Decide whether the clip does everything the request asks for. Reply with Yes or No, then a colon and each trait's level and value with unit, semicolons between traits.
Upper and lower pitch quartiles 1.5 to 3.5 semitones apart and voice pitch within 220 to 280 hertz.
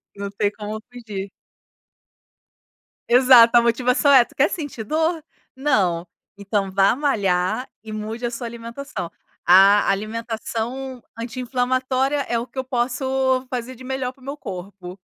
No: average, 3.9 semitones; high, 240 Hz